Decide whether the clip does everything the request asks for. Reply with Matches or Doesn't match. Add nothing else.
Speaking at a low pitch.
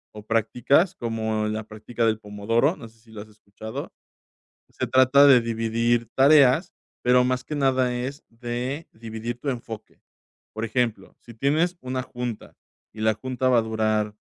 Matches